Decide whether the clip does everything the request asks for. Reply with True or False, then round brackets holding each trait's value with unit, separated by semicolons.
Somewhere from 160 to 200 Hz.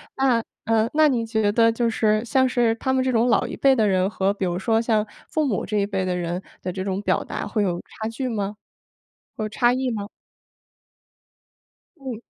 False (225 Hz)